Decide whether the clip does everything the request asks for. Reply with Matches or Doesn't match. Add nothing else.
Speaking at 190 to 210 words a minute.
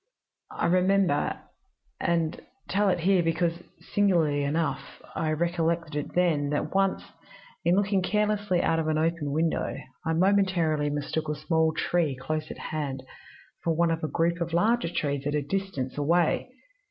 Doesn't match